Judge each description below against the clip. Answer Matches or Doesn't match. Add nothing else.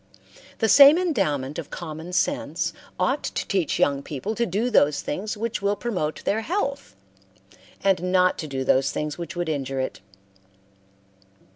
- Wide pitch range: Matches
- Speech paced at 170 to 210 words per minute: Doesn't match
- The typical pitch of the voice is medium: Matches